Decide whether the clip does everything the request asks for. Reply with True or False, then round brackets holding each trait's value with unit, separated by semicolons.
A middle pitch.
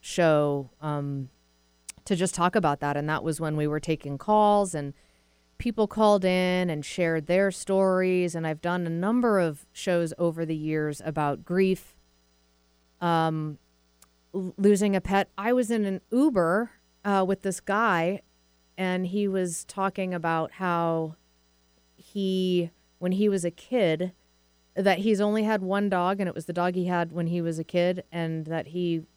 True (175 Hz)